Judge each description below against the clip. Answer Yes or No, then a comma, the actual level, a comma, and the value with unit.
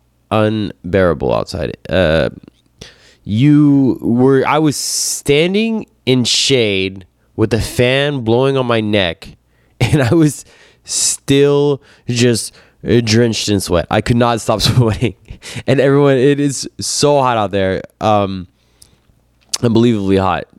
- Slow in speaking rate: Yes, slow, 120 wpm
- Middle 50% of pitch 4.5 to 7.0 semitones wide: Yes, average, 5.0 semitones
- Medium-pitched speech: No, low, 120 Hz